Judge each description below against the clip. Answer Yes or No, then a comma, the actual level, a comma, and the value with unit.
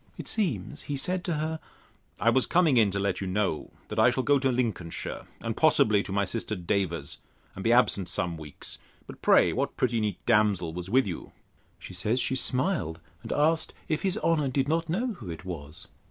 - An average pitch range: No, wide, 7.6 semitones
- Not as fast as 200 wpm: No, fast, 205 wpm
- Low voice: Yes, low, 115 Hz